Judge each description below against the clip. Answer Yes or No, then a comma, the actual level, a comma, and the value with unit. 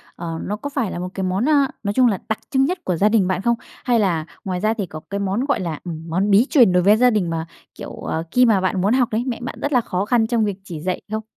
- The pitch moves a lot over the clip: No, average, 4.7 semitones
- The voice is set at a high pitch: Yes, high, 205 Hz